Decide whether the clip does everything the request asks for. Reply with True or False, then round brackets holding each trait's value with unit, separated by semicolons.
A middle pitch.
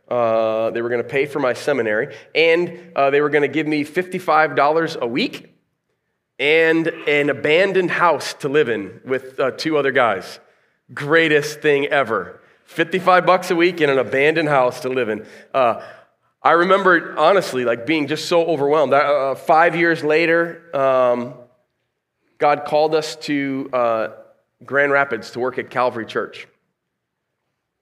True (150 Hz)